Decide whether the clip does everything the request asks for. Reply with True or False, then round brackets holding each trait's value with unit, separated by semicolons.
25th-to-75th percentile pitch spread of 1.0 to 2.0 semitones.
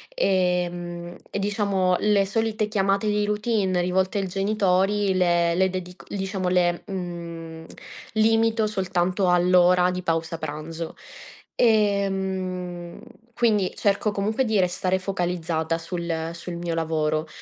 False (2.5 semitones)